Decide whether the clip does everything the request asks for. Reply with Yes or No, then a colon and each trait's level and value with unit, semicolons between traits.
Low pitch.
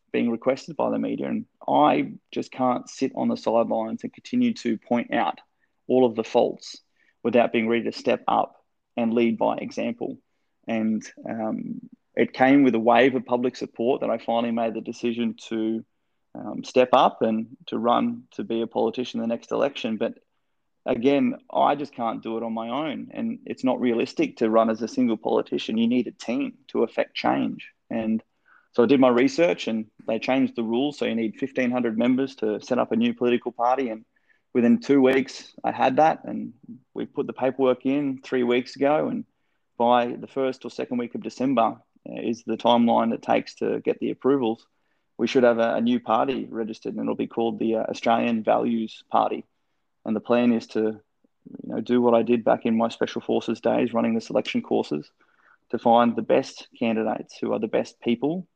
Yes: low, 120 Hz